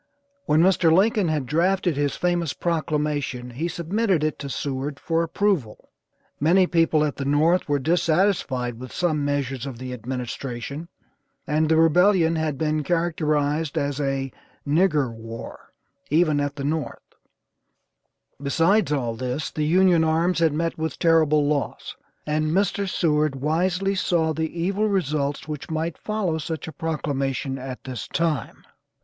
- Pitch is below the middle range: No, medium, 155 Hz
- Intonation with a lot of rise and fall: No, average, 3.2 semitones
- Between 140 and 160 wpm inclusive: Yes, average, 145 wpm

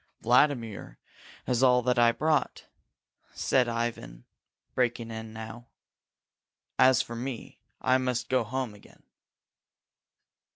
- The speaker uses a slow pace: Yes, slow, 100 wpm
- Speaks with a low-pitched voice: Yes, low, 120 Hz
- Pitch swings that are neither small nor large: No, narrow, 2.0 semitones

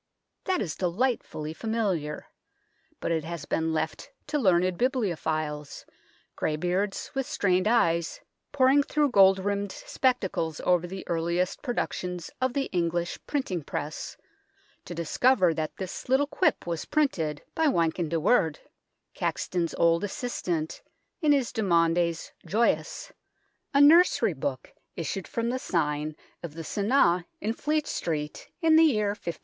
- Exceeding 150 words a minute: No, slow, 135 wpm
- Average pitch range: No, wide, 6.9 semitones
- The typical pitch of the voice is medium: Yes, medium, 180 Hz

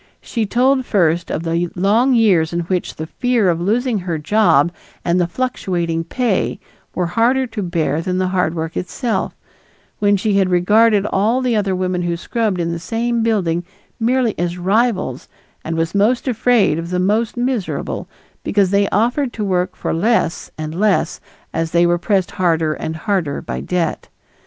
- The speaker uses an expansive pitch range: No, average, 4.8 semitones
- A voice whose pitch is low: No, high, 190 Hz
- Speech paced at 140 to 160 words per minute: No, average, 175 wpm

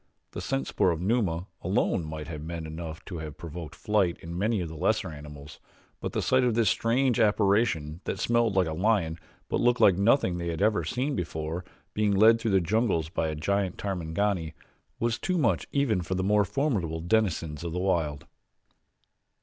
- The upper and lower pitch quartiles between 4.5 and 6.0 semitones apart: Yes, average, 5.1 semitones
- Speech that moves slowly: No, average, 190 wpm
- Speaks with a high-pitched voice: No, very low, 90 Hz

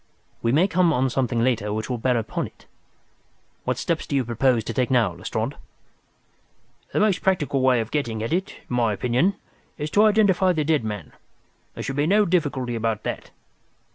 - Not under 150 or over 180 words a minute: No, average, 190 wpm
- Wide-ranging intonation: Yes, wide, 6.3 semitones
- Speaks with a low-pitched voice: Yes, low, 130 Hz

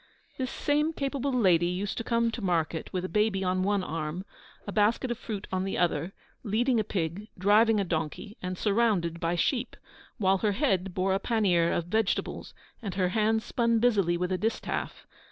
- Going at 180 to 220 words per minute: Yes, average, 190 wpm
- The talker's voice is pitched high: Yes, high, 200 Hz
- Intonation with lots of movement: No, average, 3.9 semitones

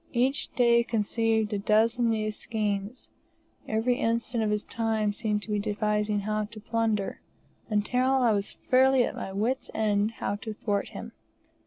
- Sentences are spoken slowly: No, average, 165 wpm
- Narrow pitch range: Yes, narrow, 1.9 semitones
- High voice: Yes, high, 220 Hz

